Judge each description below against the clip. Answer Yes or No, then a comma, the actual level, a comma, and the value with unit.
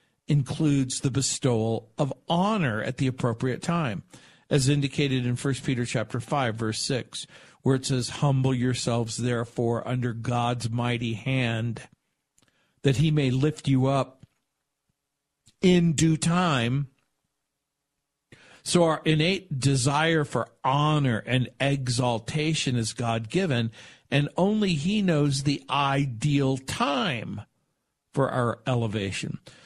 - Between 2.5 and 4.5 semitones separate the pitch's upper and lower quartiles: Yes, average, 3.1 semitones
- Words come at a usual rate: No, slow, 115 wpm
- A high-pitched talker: No, low, 135 Hz